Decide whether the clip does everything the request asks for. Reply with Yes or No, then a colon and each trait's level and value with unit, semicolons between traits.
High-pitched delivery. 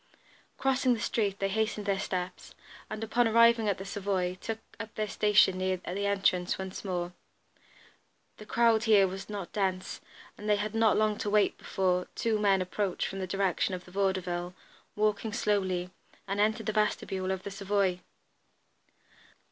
Yes: high, 200 Hz